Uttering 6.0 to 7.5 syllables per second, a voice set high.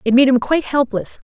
Yes: 6.1 syllables/s; very high, 260 Hz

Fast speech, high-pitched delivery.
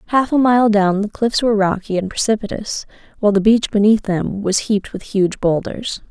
No: average, 195 wpm; high, 210 Hz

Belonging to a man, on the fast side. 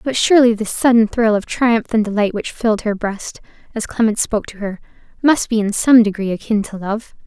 No: female; fast, 215 wpm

